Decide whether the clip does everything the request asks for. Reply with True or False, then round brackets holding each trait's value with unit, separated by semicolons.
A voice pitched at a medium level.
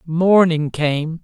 True (165 Hz)